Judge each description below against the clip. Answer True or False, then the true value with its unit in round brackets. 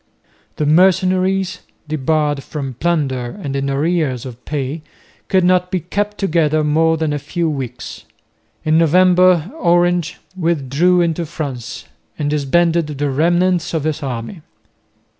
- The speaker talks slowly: True (130 wpm)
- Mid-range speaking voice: True (160 Hz)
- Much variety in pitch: False (3.6 semitones)